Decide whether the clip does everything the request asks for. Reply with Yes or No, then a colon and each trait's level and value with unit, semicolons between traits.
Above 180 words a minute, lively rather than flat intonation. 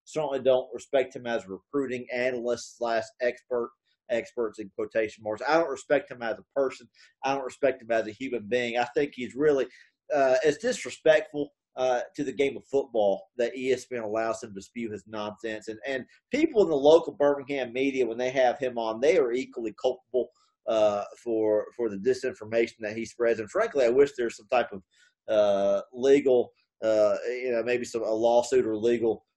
No: average, 190 wpm; average, 3.3 semitones